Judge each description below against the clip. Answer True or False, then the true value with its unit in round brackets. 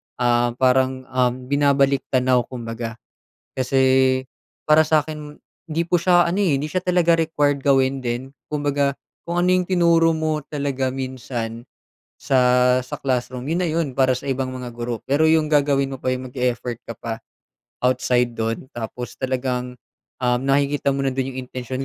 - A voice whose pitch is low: True (130 Hz)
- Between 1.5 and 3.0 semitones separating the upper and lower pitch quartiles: True (2.7 semitones)